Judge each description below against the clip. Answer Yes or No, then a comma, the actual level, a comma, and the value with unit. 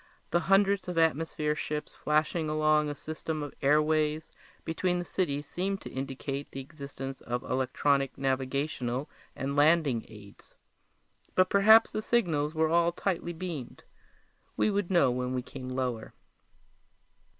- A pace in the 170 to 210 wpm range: No, average, 140 wpm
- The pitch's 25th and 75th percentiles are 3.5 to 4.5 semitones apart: Yes, average, 4.0 semitones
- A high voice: No, medium, 150 Hz